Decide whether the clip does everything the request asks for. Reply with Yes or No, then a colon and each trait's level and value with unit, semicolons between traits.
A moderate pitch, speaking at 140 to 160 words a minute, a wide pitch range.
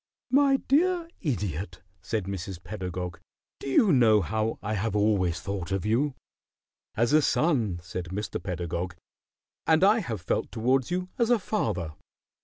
No: low, 110 Hz; average, 150 wpm; wide, 8.7 semitones